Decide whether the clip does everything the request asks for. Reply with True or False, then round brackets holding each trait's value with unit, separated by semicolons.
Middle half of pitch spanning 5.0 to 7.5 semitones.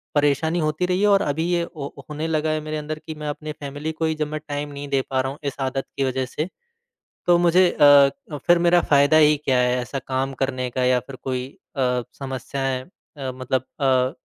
False (2.8 semitones)